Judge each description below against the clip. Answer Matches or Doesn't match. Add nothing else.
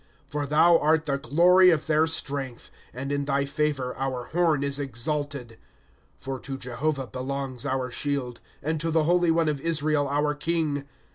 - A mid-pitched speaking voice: Matches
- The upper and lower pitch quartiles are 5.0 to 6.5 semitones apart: Doesn't match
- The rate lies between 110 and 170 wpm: Doesn't match